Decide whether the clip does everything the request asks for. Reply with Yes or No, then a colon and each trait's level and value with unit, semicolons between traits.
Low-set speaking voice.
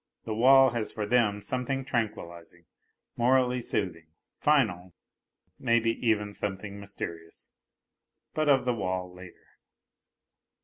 Yes: low, 110 Hz